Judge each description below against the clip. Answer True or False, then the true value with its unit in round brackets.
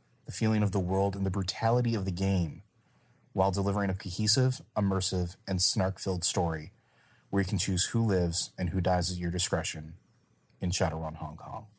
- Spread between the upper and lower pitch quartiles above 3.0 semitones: False (2.4 semitones)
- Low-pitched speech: True (95 Hz)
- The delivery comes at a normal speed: True (180 wpm)